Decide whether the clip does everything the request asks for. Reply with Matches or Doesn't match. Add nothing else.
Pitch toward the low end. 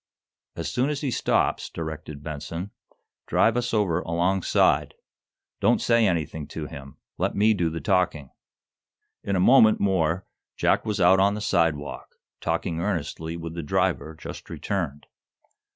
Matches